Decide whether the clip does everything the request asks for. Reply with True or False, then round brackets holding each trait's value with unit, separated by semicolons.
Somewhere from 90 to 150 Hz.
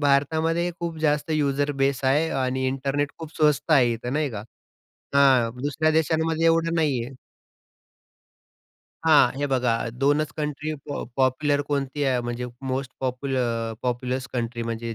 True (140 Hz)